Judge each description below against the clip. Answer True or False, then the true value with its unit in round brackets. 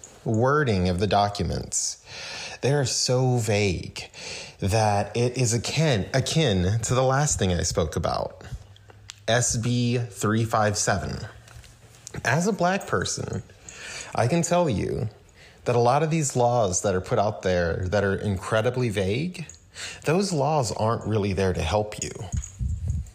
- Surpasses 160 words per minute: False (135 wpm)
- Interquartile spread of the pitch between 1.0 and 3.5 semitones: False (4.1 semitones)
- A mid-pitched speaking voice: False (110 Hz)